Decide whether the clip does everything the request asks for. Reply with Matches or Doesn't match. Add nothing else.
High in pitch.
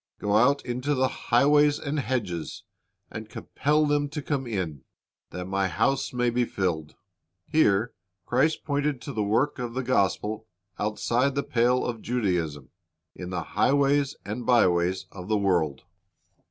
Doesn't match